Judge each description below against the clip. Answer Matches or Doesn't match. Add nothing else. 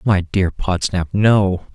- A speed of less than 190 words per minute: Matches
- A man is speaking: Matches